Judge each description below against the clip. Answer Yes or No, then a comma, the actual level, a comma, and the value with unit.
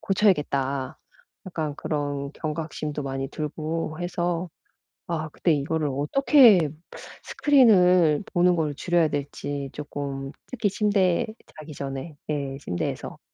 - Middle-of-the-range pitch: Yes, medium, 155 Hz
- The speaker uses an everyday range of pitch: Yes, average, 3.7 semitones